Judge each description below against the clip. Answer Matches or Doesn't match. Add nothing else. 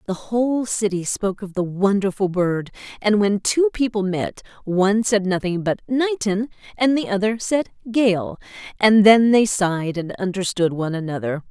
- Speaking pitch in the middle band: Doesn't match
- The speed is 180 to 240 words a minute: Doesn't match